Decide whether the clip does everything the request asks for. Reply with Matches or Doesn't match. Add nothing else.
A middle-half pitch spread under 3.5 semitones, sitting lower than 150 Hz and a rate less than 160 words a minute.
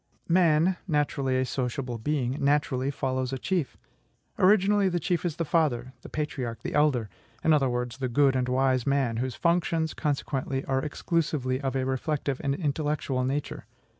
Doesn't match